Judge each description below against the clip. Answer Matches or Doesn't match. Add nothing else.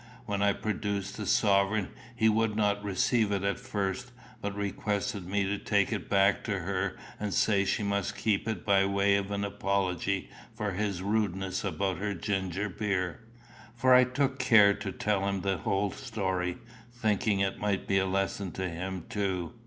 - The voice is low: Matches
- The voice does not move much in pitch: Matches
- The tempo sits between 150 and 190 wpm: Matches